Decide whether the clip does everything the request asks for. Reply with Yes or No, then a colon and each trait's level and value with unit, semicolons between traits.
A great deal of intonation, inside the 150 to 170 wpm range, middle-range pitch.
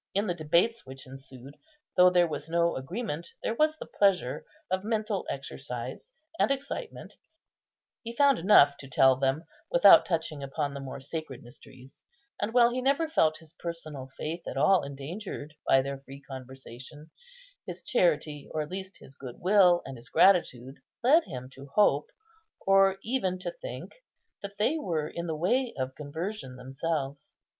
Yes: wide, 6.8 semitones; average, 165 wpm; medium, 160 Hz